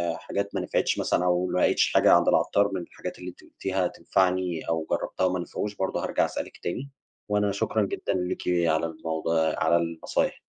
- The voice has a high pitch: No, very low, 90 Hz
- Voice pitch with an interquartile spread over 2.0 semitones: Yes, narrow, 2.5 semitones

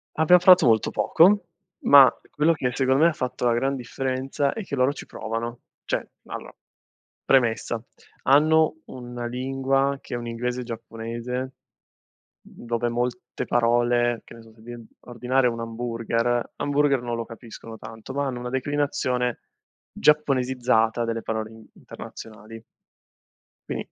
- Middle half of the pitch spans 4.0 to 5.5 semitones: No, narrow, 2.5 semitones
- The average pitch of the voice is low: Yes, low, 125 Hz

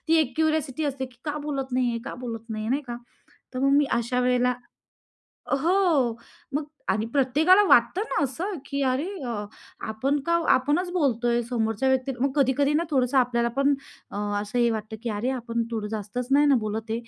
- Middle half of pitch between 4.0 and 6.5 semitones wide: No, average, 3.3 semitones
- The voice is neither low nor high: No, very high, 255 Hz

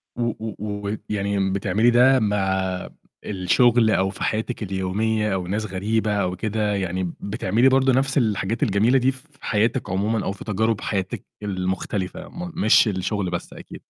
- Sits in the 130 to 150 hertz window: No, low, 105 Hz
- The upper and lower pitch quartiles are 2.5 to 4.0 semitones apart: Yes, average, 3.2 semitones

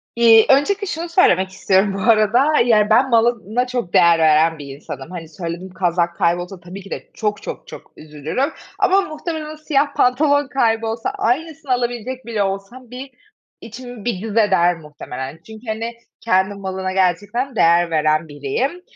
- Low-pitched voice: No, high, 215 Hz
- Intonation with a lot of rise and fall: Yes, wide, 6.2 semitones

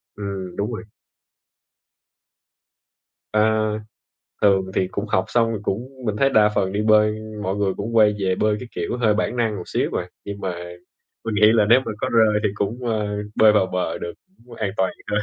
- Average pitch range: No, narrow, 1.8 semitones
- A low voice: Yes, low, 105 Hz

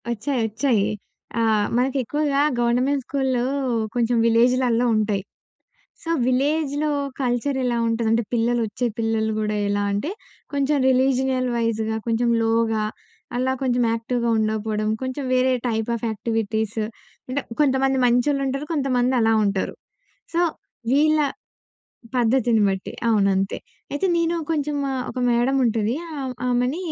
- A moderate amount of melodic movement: Yes, average, 3.1 semitones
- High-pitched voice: Yes, high, 245 Hz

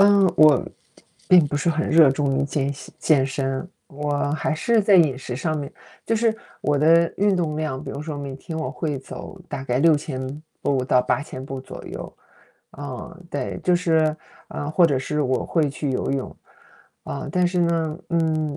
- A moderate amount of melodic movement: Yes, average, 3.4 semitones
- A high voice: No, medium, 150 Hz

